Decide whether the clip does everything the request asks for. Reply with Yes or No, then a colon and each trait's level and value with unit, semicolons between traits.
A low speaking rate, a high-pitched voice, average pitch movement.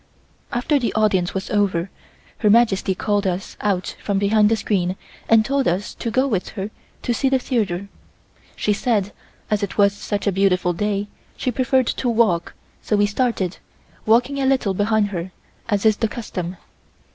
No: average, 175 wpm; high, 205 Hz; average, 3.1 semitones